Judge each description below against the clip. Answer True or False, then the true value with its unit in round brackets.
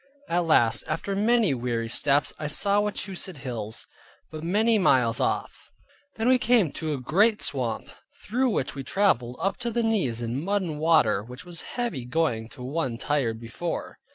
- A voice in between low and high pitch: True (155 Hz)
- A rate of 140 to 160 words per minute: False (175 wpm)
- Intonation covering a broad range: True (8.4 semitones)